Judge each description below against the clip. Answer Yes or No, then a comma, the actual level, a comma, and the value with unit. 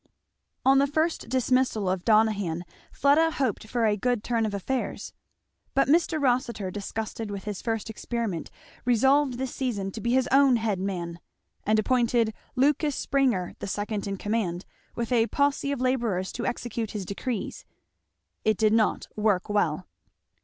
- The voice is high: Yes, high, 225 Hz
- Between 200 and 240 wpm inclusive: No, average, 155 wpm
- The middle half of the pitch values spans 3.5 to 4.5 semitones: Yes, average, 4.1 semitones